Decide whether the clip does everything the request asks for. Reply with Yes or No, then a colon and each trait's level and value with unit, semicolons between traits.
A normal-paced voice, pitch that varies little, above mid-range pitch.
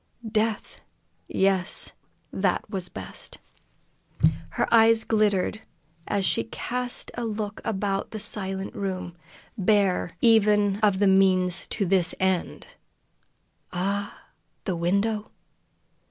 No: slow, 105 wpm; narrow, 2.2 semitones; high, 200 Hz